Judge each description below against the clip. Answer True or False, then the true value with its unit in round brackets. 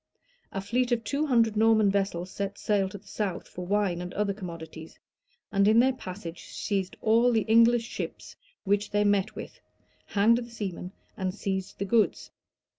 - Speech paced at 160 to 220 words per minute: True (175 wpm)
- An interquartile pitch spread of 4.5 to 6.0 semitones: False (2.9 semitones)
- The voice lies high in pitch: True (205 Hz)